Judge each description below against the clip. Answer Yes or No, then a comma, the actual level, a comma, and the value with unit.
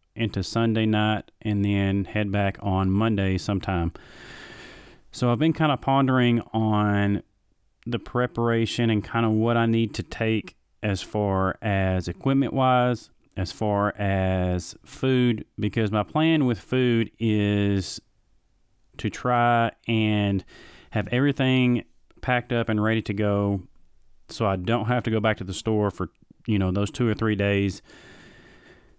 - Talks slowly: No, average, 145 wpm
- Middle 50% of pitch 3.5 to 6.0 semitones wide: No, average, 2.9 semitones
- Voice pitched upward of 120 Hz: No, low, 110 Hz